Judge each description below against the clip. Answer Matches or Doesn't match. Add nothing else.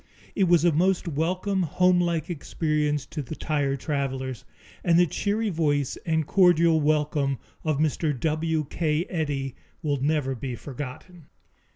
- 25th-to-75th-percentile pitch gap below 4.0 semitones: Matches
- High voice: Doesn't match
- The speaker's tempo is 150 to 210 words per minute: Doesn't match